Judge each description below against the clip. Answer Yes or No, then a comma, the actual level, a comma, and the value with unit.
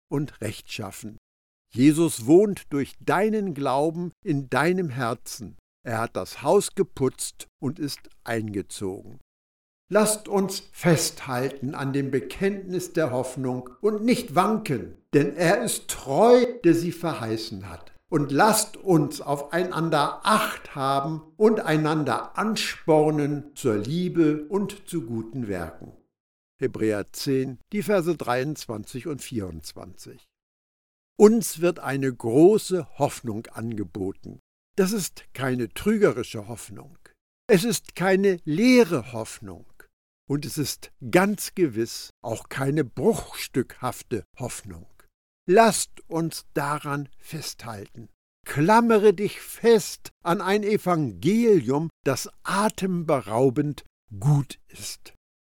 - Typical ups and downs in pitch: No, wide, 7.5 semitones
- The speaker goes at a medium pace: No, slow, 105 wpm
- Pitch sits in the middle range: Yes, medium, 145 Hz